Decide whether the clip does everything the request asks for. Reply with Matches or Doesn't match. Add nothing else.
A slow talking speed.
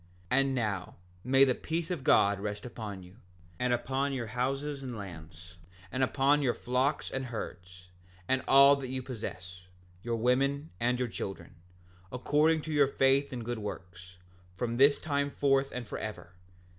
Doesn't match